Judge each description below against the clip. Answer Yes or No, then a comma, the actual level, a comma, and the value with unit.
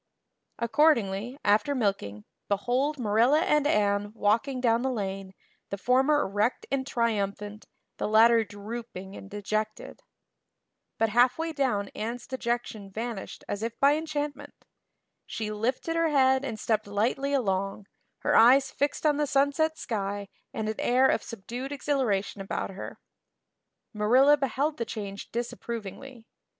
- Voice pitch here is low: No, high, 230 Hz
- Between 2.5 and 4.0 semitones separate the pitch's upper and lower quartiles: No, average, 4.8 semitones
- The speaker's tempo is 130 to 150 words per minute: Yes, slow, 135 wpm